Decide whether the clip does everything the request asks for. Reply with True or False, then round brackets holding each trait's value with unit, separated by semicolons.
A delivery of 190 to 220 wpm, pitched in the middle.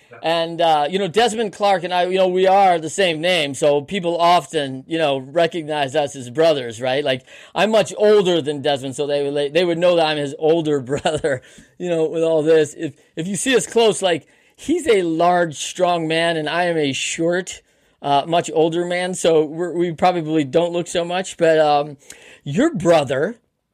True (200 wpm; 165 Hz)